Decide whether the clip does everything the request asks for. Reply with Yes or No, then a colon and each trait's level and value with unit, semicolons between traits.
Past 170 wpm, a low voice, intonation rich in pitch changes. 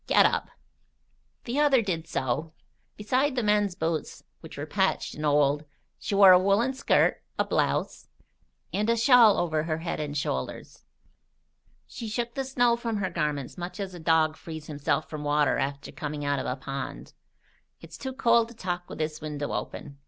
No: average, 180 wpm; medium, 170 Hz; wide, 7.2 semitones